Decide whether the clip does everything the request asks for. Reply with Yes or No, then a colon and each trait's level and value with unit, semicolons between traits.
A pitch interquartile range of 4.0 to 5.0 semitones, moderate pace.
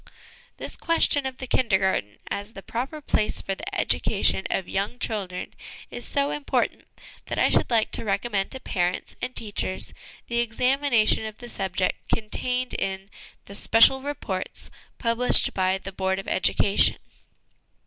Yes: average, 4.6 semitones; average, 150 wpm